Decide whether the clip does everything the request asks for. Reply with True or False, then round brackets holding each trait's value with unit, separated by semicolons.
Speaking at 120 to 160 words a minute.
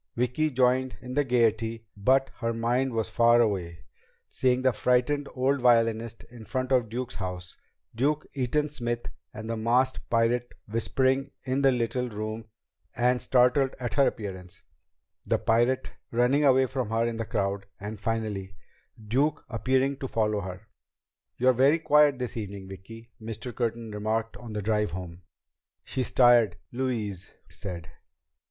True (150 wpm)